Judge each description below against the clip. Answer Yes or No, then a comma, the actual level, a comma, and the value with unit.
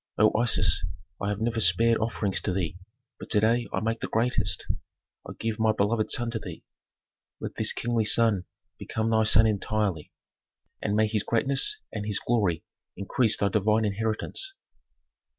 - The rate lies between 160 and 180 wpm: Yes, average, 165 wpm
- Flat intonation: Yes, narrow, 1.9 semitones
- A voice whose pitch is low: Yes, low, 110 Hz